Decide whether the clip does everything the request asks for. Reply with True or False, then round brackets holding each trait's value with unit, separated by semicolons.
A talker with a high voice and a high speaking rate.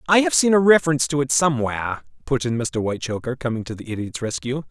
False (135 Hz; 215 wpm)